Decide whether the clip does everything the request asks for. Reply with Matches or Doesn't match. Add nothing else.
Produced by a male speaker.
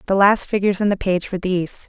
Doesn't match